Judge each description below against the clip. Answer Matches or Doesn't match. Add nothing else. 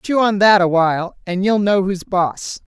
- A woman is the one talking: Matches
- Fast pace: Matches